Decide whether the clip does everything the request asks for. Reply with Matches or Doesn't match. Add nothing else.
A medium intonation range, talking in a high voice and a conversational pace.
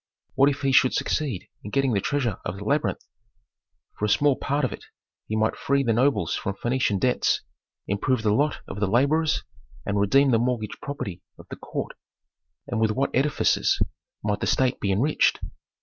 Doesn't match